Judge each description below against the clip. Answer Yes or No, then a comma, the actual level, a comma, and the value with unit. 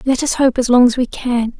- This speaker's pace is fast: Yes, fast, 300 wpm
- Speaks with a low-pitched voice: No, very high, 250 Hz